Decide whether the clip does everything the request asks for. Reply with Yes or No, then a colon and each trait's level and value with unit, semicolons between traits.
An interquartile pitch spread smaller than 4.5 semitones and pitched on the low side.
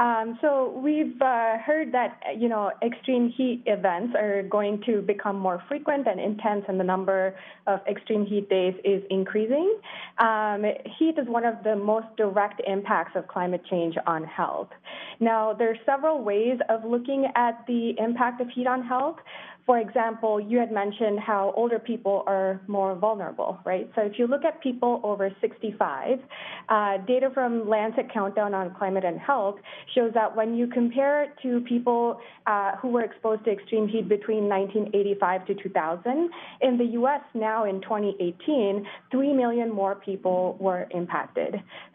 No: average, 3.5 semitones; high, 220 Hz